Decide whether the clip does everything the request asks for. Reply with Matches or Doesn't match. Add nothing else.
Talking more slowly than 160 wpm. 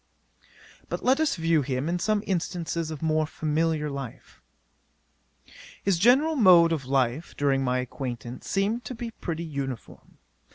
Matches